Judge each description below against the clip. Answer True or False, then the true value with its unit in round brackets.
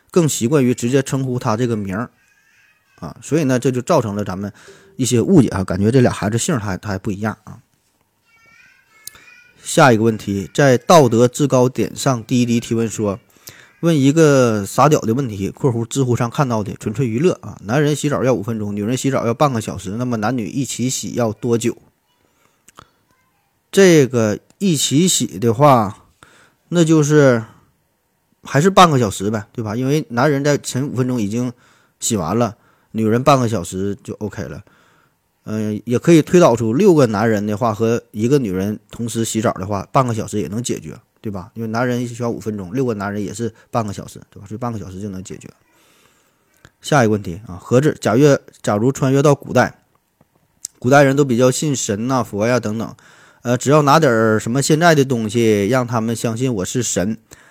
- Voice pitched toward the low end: True (120 Hz)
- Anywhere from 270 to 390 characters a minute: True (280 characters per minute)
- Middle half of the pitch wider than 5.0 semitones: False (4.3 semitones)